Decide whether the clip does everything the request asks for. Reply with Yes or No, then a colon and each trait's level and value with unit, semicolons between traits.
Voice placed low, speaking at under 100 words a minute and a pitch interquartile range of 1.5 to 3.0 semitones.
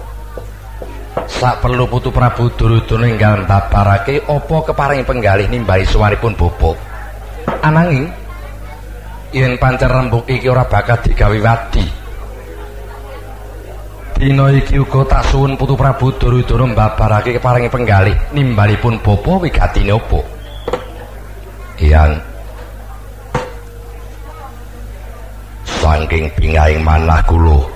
No: low, 105 Hz; average, 90 wpm; average, 3.9 semitones